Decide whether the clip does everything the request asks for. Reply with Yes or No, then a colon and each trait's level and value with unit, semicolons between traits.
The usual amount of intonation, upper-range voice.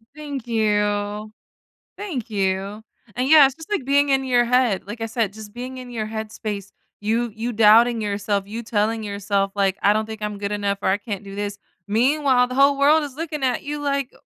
Yes: average, 4.1 semitones; high, 225 Hz